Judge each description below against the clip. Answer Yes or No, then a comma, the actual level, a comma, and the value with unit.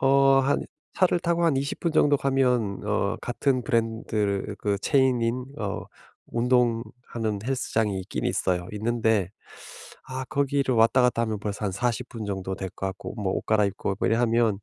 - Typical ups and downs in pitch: Yes, average, 3.8 semitones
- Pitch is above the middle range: No, low, 115 Hz